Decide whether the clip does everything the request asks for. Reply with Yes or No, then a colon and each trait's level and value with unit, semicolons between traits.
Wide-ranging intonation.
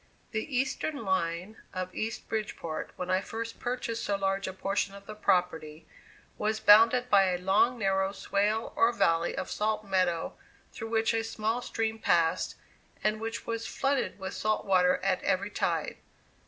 No: average, 3.1 semitones